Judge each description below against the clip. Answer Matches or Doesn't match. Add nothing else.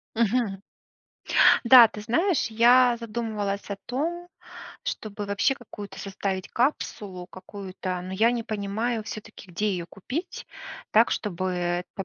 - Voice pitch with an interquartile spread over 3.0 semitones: Matches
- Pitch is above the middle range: Matches